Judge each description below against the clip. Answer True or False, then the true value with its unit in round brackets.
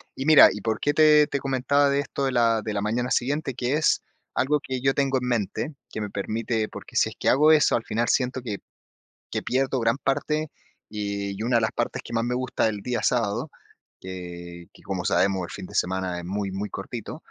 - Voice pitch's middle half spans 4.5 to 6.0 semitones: True (4.8 semitones)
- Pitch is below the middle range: True (120 Hz)